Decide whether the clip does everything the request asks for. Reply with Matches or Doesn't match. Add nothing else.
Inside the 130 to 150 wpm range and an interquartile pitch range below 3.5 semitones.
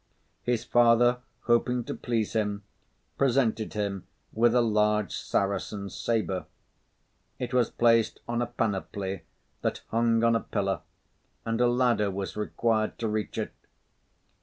Matches